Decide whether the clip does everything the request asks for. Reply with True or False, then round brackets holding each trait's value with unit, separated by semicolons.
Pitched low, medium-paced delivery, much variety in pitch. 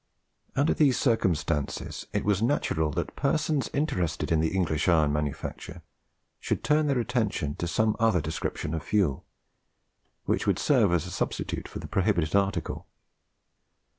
True (95 Hz; 145 wpm; 7.8 semitones)